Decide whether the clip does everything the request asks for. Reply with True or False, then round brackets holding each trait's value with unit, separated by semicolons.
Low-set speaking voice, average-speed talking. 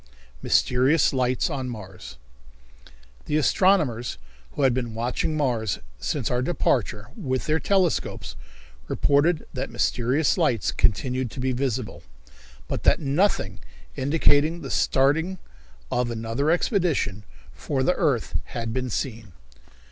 False (130 Hz; 120 wpm)